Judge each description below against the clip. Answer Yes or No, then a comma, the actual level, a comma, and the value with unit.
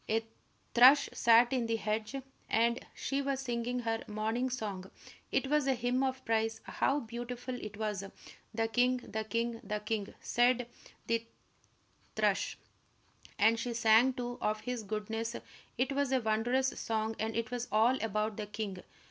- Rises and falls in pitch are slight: Yes, narrow, 2.2 semitones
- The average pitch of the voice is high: Yes, high, 230 Hz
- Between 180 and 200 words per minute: No, average, 160 wpm